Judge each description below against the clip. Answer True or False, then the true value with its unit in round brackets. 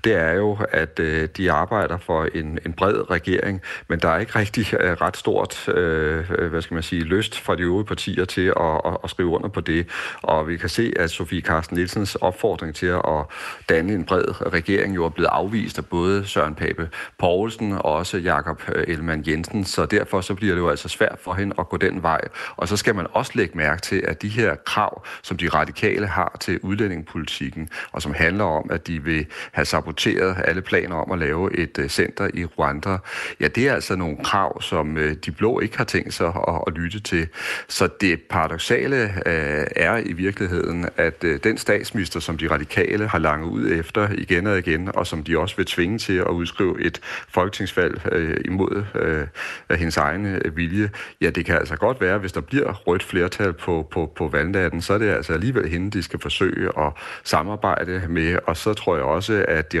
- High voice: False (85 Hz)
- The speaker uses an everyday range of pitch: True (3.3 semitones)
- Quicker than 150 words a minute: True (200 wpm)